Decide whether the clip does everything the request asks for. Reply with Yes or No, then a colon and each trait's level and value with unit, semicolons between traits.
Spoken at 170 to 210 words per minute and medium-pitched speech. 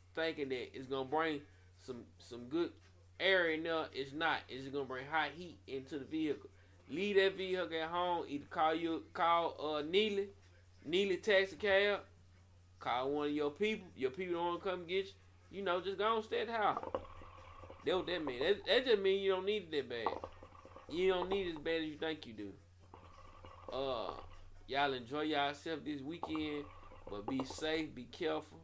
Yes: average, 200 wpm; medium, 155 Hz